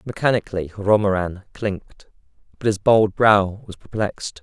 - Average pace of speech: No, slow, 120 wpm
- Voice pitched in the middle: No, low, 100 Hz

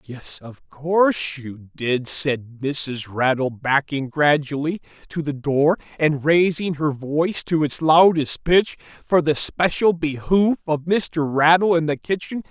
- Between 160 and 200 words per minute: No, average, 150 wpm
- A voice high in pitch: No, medium, 150 Hz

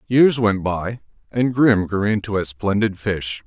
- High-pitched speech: No, low, 100 Hz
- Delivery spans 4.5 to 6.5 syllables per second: No, 4.0 syllables/s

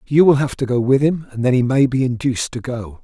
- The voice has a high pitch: No, low, 130 Hz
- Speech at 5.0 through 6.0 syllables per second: Yes, 5.9 syllables/s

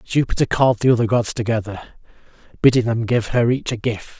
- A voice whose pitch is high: No, low, 115 Hz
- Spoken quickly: No, average, 185 wpm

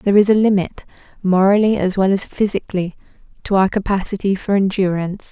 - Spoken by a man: No, female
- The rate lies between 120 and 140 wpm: No, average, 160 wpm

